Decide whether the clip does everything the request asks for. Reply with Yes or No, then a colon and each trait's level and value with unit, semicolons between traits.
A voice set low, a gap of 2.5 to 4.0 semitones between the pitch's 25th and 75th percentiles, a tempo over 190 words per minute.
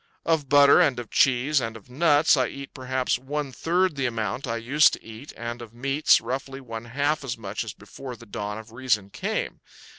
Yes: low, 130 Hz; average, 3.6 semitones; fast, 205 wpm